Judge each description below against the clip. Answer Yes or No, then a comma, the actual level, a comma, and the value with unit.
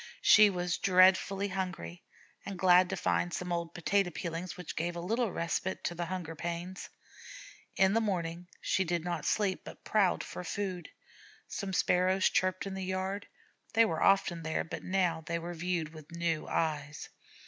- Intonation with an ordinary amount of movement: No, narrow, 2.1 semitones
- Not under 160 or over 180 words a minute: Yes, average, 170 wpm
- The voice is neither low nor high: Yes, medium, 180 Hz